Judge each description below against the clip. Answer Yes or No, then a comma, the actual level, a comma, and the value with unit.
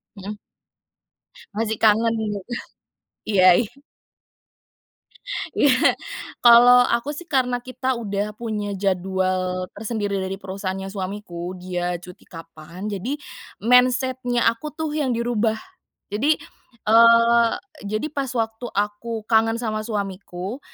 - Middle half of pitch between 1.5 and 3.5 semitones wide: No, average, 3.9 semitones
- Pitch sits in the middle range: No, high, 220 Hz